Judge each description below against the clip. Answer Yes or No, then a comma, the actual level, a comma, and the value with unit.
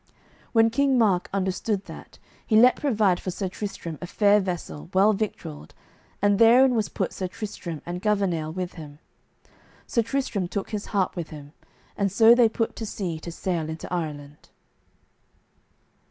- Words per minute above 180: No, average, 160 wpm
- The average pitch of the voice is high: Yes, high, 195 Hz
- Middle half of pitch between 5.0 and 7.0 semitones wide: No, average, 4.2 semitones